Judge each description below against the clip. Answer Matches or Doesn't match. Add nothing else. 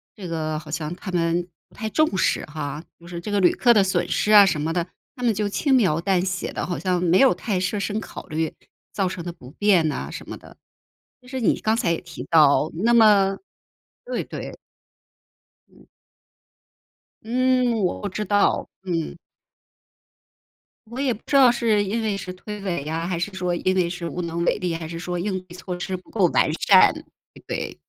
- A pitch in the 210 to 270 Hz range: Doesn't match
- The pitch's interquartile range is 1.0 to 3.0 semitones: Doesn't match